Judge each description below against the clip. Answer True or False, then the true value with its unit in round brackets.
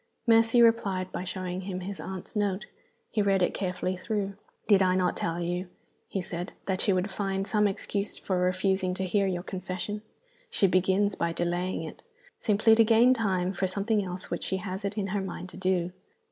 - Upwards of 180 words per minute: True (195 wpm)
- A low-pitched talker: False (190 Hz)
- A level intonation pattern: True (1.9 semitones)